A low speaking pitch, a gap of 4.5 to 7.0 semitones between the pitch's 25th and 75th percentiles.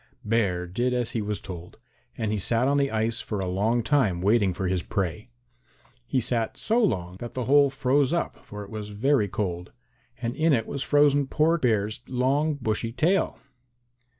Yes: low, 115 Hz; average, 5.1 semitones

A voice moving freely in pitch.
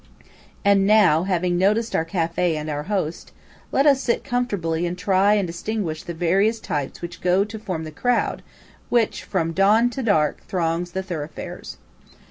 No: average, 4.2 semitones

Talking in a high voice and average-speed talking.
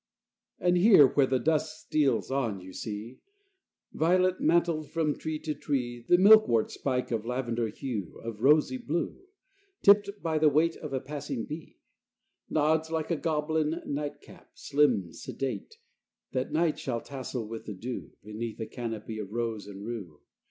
No: low, 135 Hz; average, 160 wpm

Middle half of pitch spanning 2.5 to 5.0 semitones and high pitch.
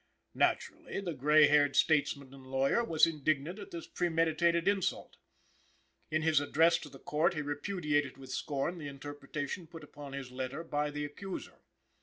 No: average, 2.8 semitones; medium, 150 Hz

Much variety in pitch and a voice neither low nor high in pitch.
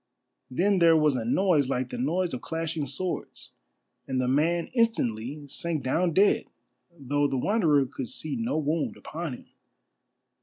No: average, 4.5 semitones; medium, 155 Hz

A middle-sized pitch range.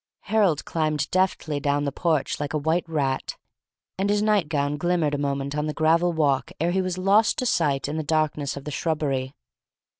Yes: average, 3.4 semitones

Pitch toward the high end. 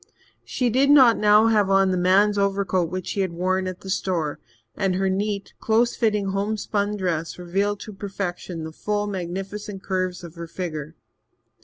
Yes: high, 195 Hz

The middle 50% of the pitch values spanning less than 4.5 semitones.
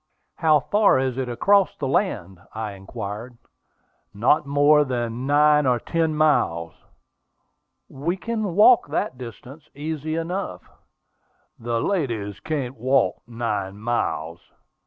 No: average, 5.3 semitones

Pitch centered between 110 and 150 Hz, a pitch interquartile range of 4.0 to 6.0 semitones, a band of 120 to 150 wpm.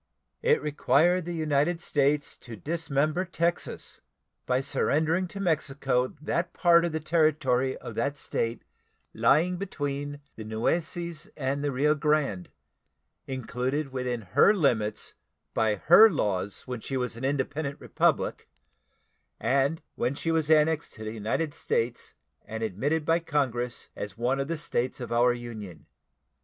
Yes: medium, 140 Hz; average, 4.7 semitones; average, 140 wpm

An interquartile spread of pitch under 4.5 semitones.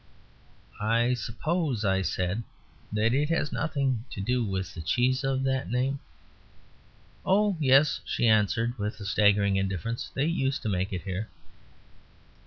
No: average, 5.0 semitones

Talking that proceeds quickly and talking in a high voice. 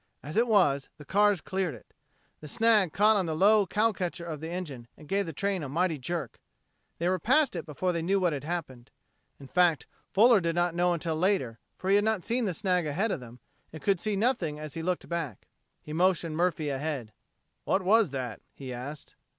No: fast, 220 wpm; medium, 175 Hz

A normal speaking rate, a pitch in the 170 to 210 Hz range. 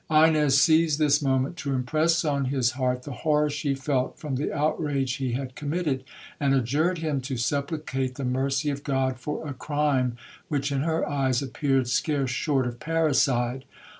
No: average, 170 wpm; medium, 140 Hz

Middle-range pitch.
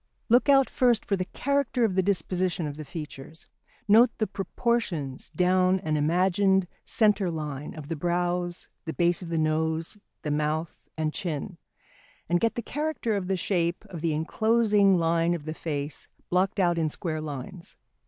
Yes: medium, 175 Hz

